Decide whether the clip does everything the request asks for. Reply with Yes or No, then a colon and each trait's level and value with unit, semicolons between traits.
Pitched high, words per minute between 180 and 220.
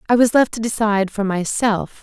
Yes: high, 215 Hz; fast, 205 wpm